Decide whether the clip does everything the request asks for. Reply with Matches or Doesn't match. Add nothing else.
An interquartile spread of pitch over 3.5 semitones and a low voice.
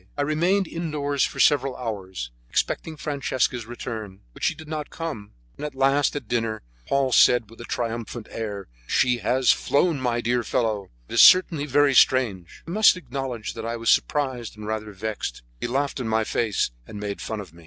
Matches